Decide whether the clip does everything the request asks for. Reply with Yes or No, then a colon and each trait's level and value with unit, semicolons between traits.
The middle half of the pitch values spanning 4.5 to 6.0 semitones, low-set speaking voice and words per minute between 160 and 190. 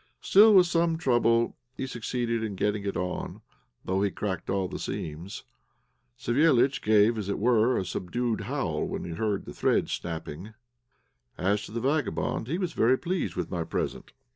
Yes: average, 5.1 semitones; low, 110 Hz; average, 170 wpm